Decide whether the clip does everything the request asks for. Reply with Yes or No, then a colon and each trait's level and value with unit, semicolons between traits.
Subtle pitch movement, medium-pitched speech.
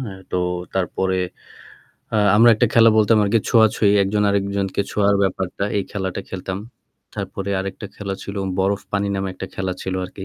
No: narrow, 1.5 semitones; low, 100 Hz